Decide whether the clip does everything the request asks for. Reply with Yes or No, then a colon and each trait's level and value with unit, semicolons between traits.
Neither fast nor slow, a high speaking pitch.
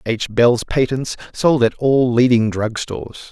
No: average, 165 wpm; low, 120 Hz